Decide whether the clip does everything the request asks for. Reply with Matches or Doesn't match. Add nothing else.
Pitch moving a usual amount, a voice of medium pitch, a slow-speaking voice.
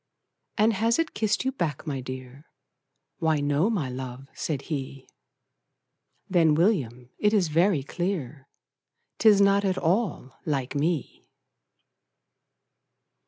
Doesn't match